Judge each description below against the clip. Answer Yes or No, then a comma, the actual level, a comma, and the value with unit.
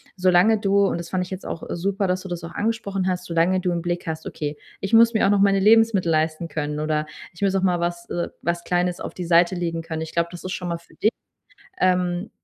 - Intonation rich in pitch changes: No, narrow, 2.4 semitones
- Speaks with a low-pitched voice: No, medium, 175 Hz